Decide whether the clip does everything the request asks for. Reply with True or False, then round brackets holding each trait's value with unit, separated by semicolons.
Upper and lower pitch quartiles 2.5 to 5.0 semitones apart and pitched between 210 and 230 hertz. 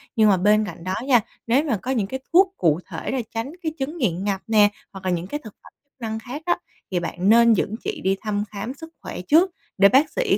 False (5.6 semitones; 220 Hz)